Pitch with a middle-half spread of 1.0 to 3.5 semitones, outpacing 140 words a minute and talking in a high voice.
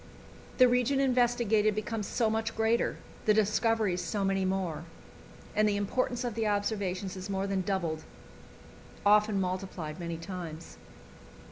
No: average, 3.1 semitones; slow, 135 wpm; high, 205 Hz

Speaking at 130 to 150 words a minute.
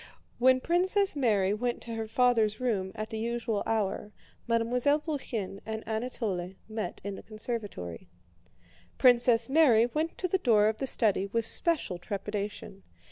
Yes: average, 145 wpm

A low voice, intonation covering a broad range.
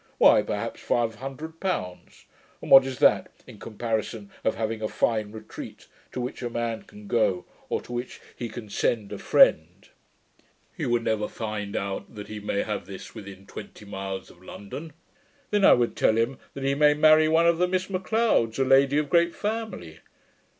Yes: low, 120 Hz; wide, 5.9 semitones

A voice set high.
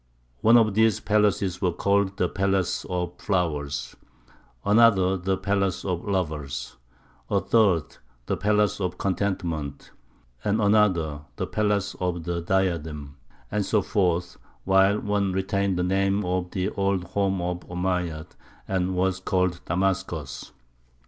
No: very low, 95 Hz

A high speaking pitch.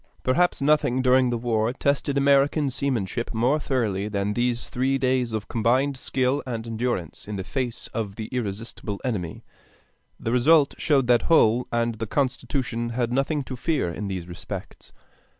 No: low, 125 Hz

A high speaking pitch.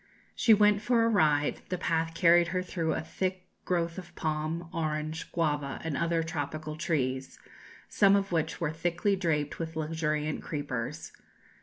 No: medium, 165 Hz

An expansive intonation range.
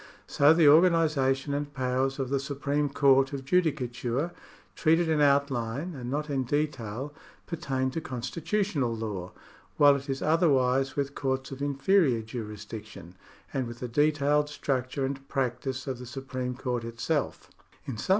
No: average, 2.7 semitones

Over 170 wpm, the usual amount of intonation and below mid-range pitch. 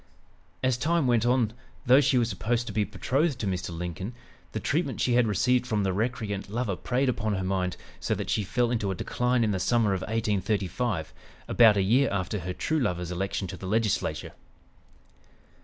Yes: average, 190 wpm; average, 4.3 semitones; low, 110 Hz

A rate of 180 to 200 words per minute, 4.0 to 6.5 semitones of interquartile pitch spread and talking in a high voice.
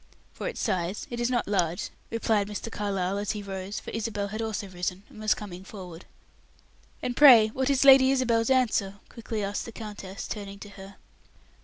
No: average, 185 wpm; average, 2.8 semitones; high, 210 Hz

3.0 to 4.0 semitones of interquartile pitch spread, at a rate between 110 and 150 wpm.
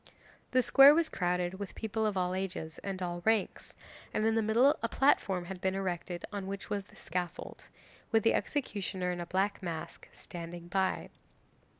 No: average, 3.5 semitones; average, 180 wpm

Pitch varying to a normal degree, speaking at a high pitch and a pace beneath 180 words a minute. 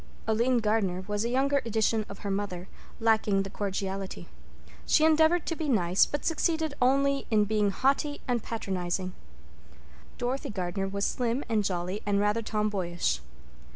Yes: average, 4.7 semitones; high, 215 Hz; average, 150 wpm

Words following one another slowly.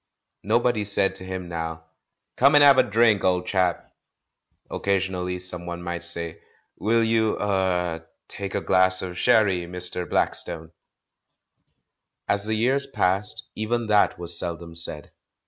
No: average, 150 wpm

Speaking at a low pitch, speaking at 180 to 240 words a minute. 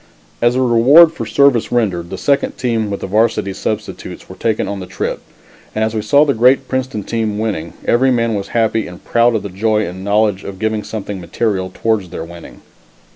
Yes: low, 110 Hz; fast, 205 wpm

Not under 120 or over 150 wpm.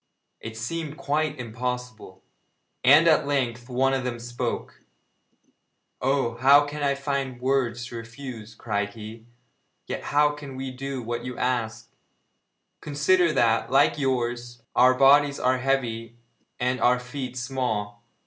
Yes: slow, 135 wpm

